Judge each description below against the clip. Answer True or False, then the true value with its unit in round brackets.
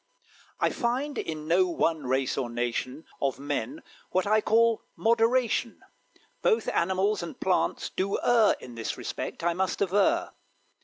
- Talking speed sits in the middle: True (145 wpm)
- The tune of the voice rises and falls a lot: True (7.2 semitones)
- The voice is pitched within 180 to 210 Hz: True (185 Hz)